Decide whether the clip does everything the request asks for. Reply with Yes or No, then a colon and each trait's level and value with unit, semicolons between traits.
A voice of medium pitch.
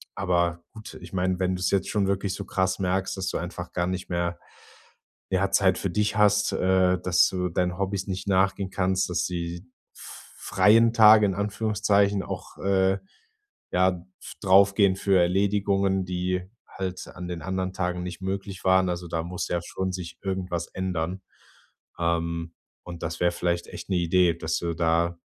No: very low, 95 Hz